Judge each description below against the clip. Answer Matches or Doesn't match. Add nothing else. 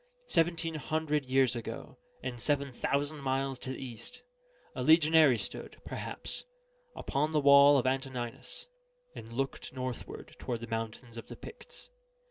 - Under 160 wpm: Matches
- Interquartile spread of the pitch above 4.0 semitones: Doesn't match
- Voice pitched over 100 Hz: Matches